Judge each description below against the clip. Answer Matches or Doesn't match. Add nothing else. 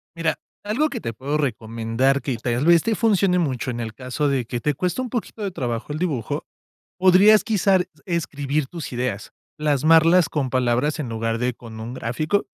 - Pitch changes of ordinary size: Doesn't match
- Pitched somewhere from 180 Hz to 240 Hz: Doesn't match